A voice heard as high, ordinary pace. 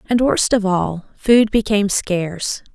Yes: high, 205 Hz; average, 155 wpm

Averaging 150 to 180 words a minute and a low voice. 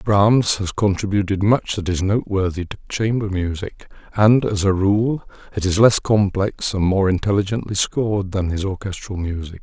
Yes: average, 160 wpm; low, 100 Hz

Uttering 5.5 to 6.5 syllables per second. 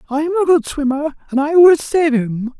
Yes: 5.9 syllables/s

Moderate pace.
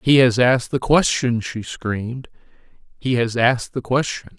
Yes: average, 150 wpm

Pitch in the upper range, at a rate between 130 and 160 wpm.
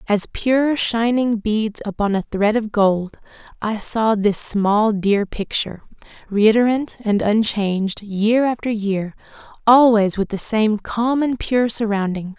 Yes: high, 215 Hz; average, 140 wpm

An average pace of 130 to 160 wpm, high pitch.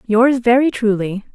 Yes: slow, 135 wpm; high, 230 Hz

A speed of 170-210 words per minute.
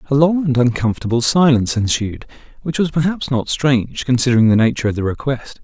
Yes: average, 180 wpm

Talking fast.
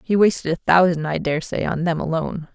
Yes: fast, 210 wpm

